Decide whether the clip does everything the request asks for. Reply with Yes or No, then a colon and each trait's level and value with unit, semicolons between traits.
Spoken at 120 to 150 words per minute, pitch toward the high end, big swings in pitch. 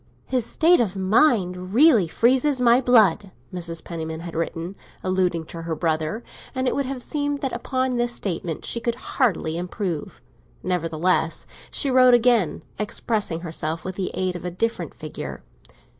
No: average, 160 wpm; high, 195 Hz; wide, 6.6 semitones